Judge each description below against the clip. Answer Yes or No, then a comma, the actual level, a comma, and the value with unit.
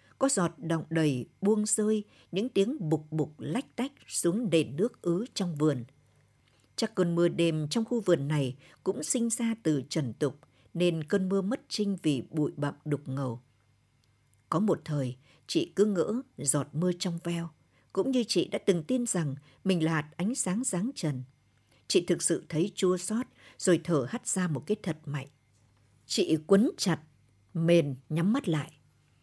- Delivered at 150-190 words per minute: Yes, average, 180 wpm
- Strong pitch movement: Yes, wide, 5.9 semitones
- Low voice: No, medium, 165 Hz